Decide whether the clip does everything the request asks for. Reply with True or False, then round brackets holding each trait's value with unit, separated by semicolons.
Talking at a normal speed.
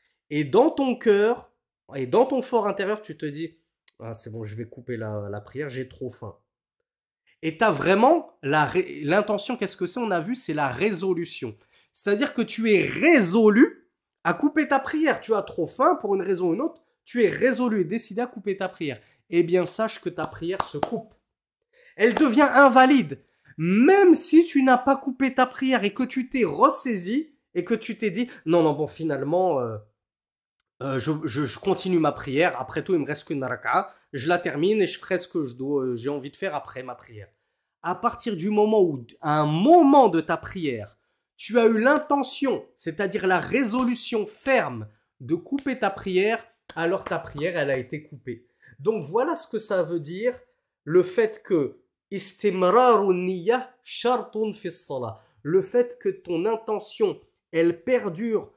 True (180 wpm)